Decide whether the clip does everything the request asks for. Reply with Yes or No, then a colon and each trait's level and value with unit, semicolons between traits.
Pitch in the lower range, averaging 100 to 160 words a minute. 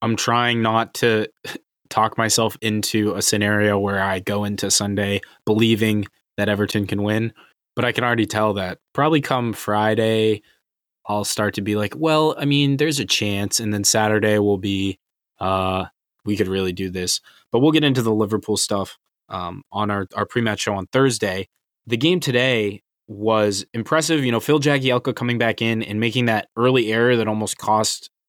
No: low, 110 Hz; average, 180 wpm